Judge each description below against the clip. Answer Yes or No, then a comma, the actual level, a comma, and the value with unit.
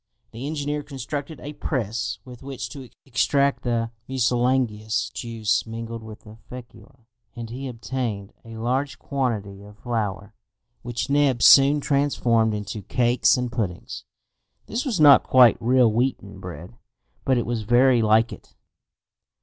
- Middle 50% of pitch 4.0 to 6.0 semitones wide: No, average, 3.1 semitones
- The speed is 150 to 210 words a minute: No, average, 140 wpm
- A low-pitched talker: Yes, low, 120 Hz